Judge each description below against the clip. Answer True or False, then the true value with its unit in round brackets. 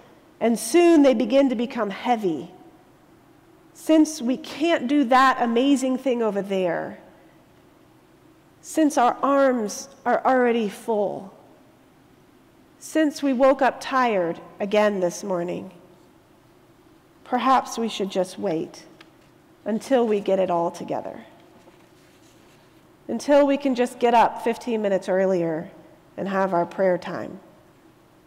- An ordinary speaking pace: False (115 wpm)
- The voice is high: True (240 Hz)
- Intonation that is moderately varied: False (5.7 semitones)